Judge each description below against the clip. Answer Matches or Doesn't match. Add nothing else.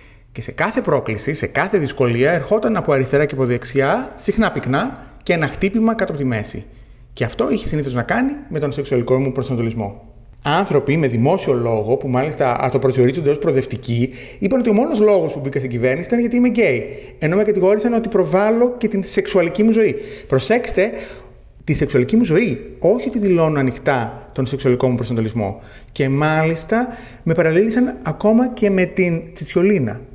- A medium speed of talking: Doesn't match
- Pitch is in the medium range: Matches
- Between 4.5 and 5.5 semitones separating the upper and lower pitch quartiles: Doesn't match